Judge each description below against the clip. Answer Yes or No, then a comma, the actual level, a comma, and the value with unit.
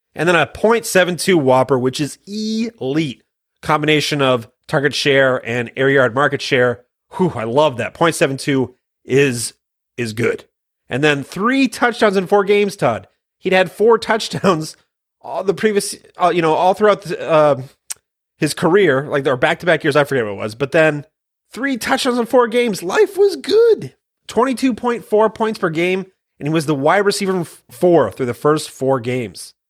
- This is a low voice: No, medium, 165 Hz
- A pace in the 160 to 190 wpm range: Yes, average, 170 wpm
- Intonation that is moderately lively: No, wide, 7.6 semitones